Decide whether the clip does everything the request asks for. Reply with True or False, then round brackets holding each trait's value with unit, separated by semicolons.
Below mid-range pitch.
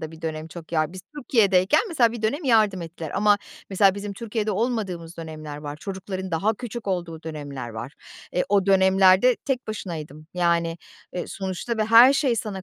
False (190 Hz)